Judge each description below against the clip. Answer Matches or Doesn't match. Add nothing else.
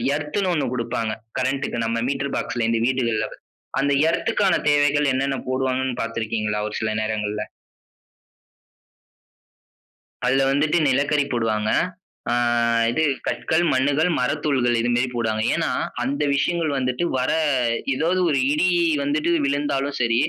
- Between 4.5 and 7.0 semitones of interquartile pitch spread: Doesn't match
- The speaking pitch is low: Matches